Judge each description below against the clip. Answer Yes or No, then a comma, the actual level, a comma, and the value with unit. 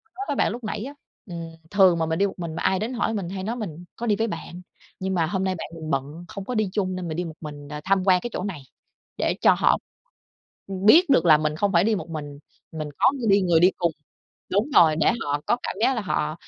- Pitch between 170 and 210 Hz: Yes, medium, 185 Hz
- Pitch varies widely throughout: No, average, 4.2 semitones